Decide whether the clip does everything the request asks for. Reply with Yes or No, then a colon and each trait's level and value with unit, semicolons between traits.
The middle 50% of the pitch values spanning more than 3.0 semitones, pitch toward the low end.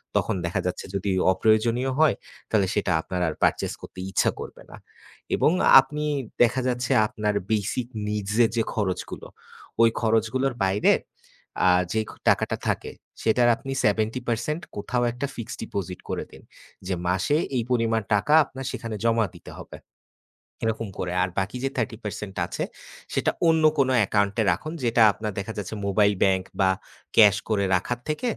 Yes: average, 3.5 semitones; low, 110 Hz